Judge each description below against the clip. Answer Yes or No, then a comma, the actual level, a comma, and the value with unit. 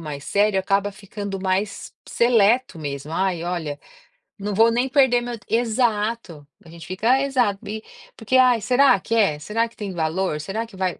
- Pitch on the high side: Yes, high, 205 Hz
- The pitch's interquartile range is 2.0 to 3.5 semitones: No, average, 4.1 semitones